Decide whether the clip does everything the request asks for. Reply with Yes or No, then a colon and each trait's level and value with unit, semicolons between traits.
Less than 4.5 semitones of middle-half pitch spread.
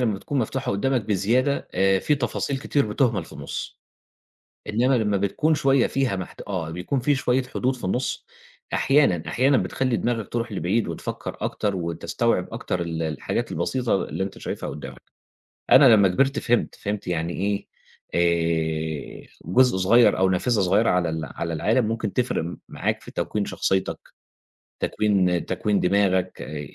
No: wide, 5.5 semitones